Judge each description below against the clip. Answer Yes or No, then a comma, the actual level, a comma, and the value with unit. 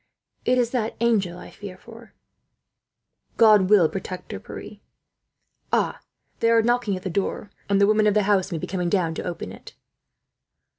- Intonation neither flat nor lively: Yes, average, 3.5 semitones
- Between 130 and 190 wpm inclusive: Yes, average, 180 wpm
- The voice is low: No, high, 205 Hz